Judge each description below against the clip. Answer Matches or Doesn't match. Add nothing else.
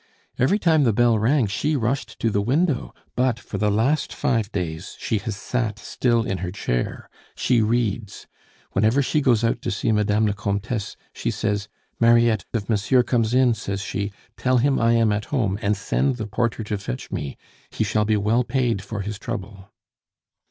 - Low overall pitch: Matches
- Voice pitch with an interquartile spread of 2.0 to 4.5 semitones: Matches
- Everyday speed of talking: Matches